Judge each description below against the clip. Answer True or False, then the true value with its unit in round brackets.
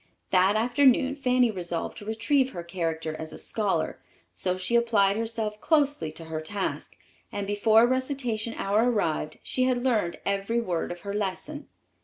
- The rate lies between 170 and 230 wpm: False (160 wpm)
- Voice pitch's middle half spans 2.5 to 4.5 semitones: False (4.9 semitones)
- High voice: True (215 Hz)